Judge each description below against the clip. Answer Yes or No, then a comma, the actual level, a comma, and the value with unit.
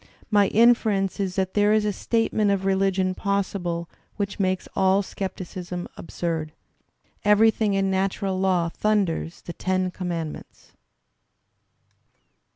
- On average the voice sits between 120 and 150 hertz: No, high, 190 Hz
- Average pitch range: No, narrow, 2.0 semitones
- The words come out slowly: Yes, slow, 115 wpm